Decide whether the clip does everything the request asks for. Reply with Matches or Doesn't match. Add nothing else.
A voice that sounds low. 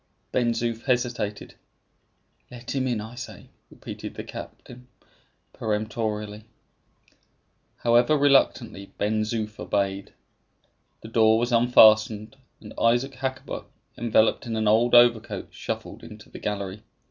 Matches